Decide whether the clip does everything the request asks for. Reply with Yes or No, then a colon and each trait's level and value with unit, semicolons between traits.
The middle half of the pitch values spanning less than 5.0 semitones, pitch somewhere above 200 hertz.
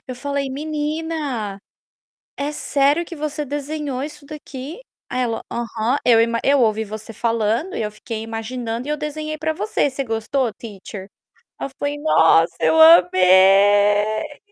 No: average, 5.3 semitones; high, 245 Hz